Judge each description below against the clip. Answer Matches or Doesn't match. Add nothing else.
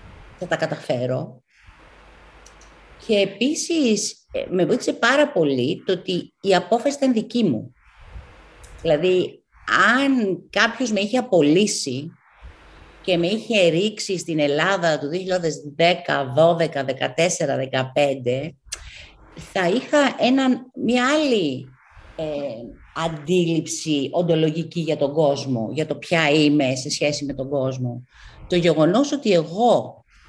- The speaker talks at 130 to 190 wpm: Doesn't match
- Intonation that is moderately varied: Doesn't match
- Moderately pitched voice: Matches